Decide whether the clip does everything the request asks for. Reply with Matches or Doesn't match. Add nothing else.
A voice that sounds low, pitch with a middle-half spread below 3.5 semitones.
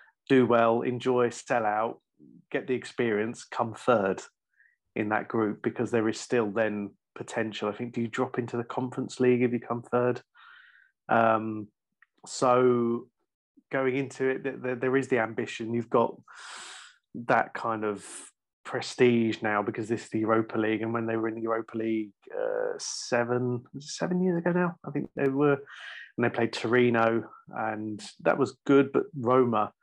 Matches